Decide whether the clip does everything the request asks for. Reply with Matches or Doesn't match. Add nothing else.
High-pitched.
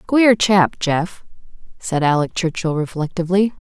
Doesn't match